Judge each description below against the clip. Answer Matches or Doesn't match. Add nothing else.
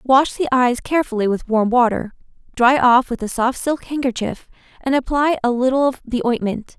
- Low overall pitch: Doesn't match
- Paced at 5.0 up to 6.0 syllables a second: Matches